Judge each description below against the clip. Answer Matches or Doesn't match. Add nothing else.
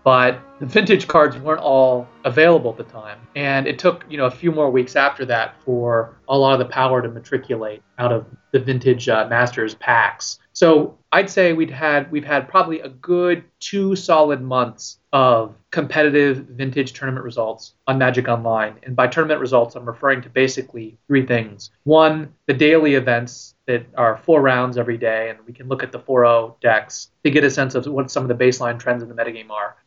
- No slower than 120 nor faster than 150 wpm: Doesn't match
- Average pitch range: Matches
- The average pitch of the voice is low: Matches